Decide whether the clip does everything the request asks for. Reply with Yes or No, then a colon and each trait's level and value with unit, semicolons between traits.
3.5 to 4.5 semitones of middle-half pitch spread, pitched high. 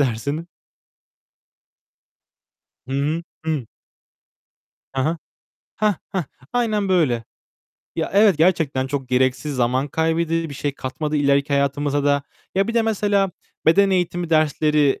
No: average, 4.1 semitones; medium, 150 Hz